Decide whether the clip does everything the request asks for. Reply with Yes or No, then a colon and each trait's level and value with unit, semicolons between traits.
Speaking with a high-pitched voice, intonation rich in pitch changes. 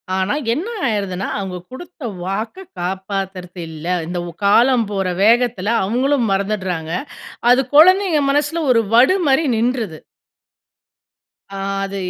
Yes: high, 215 Hz; wide, 5.7 semitones